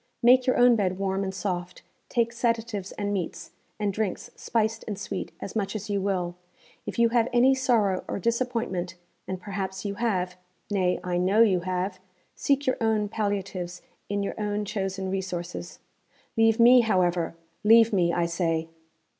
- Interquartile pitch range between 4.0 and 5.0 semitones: No, average, 3.6 semitones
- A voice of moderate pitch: No, high, 200 Hz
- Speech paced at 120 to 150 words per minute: No, average, 165 wpm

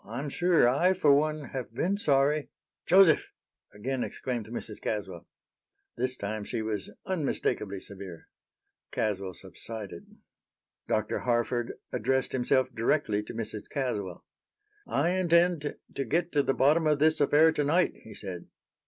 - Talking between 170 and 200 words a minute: No, slow, 135 wpm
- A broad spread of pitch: Yes, wide, 6.1 semitones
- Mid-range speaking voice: No, low, 130 Hz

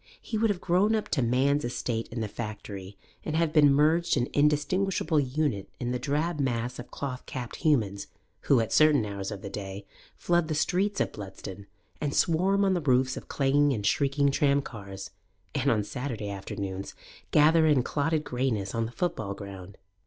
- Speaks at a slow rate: No, average, 180 wpm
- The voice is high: No, low, 135 Hz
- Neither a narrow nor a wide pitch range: No, wide, 6.4 semitones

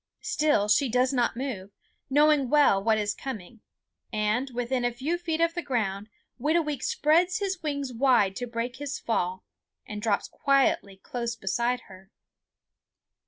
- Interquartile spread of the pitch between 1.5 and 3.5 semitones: No, average, 5.3 semitones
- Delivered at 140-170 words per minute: Yes, average, 155 wpm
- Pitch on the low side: No, high, 245 Hz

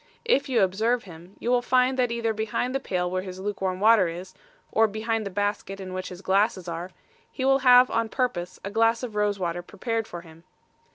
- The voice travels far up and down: No, average, 4.1 semitones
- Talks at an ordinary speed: No, fast, 220 wpm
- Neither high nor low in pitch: No, high, 210 Hz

